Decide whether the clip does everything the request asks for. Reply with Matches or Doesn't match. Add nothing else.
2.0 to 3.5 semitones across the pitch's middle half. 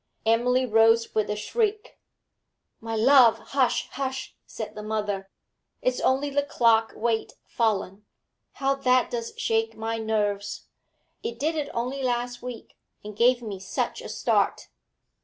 Matches